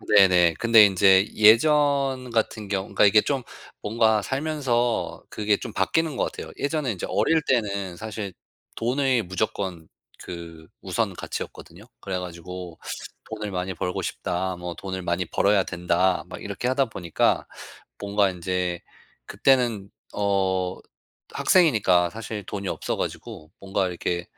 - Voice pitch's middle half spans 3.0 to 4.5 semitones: Yes, average, 4.2 semitones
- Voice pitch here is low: Yes, low, 100 Hz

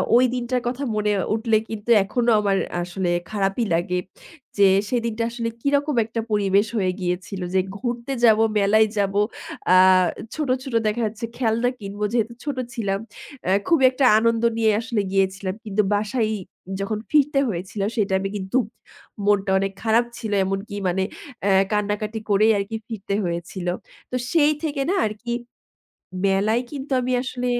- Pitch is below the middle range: No, high, 215 Hz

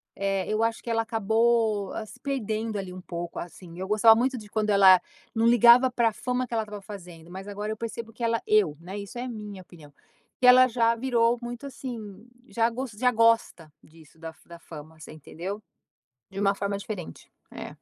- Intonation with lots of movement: No, average, 3.5 semitones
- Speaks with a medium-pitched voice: No, high, 215 Hz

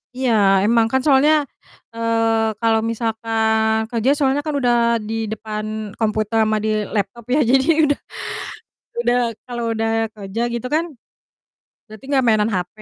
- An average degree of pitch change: No, narrow, 2.3 semitones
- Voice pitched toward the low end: No, high, 225 Hz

